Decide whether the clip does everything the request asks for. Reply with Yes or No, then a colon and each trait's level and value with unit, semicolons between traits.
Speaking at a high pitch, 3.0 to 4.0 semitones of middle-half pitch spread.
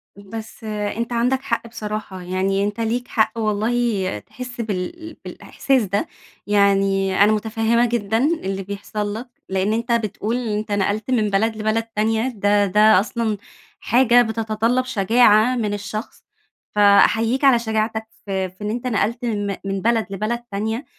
No: high, 215 Hz; narrow, 2.4 semitones